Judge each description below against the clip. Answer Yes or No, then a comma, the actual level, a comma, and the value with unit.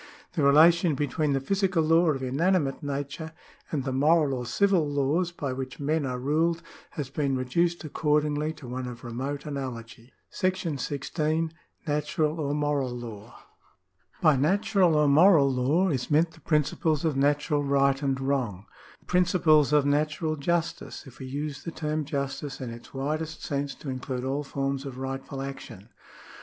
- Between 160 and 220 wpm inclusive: Yes, average, 165 wpm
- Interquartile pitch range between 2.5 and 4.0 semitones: Yes, average, 2.8 semitones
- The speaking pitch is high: No, medium, 145 Hz